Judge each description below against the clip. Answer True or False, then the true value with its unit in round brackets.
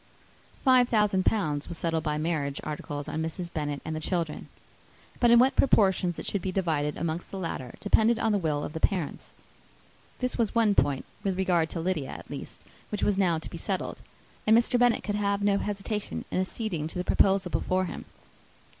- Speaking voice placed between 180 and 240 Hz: True (185 Hz)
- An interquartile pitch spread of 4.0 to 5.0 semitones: True (4.6 semitones)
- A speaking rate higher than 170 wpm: True (200 wpm)